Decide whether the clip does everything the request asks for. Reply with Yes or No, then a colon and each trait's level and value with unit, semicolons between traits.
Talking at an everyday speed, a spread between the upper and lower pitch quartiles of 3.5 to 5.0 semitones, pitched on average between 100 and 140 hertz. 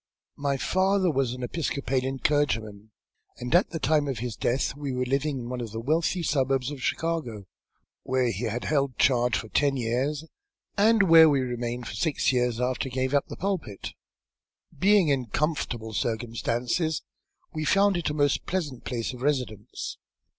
Yes: average, 175 wpm; average, 4.1 semitones; low, 135 Hz